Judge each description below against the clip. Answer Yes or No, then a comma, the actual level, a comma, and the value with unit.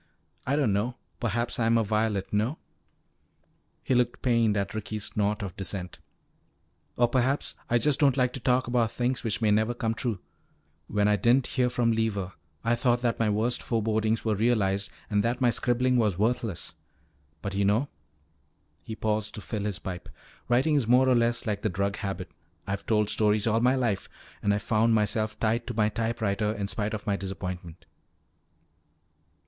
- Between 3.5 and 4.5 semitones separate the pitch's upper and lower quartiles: No, average, 2.8 semitones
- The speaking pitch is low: Yes, low, 110 Hz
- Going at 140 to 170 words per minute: No, average, 180 wpm